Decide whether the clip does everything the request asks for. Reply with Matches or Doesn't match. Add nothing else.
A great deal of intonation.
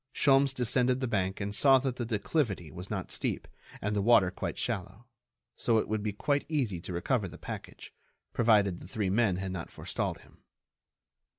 Doesn't match